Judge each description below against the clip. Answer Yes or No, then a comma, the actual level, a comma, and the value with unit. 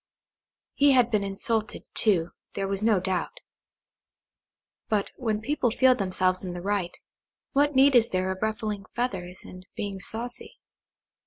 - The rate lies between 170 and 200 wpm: No, average, 145 wpm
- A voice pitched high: Yes, high, 210 Hz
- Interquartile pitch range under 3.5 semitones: No, average, 4.3 semitones